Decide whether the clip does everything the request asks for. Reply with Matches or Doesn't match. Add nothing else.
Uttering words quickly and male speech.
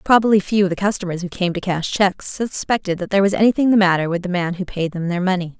Doesn't match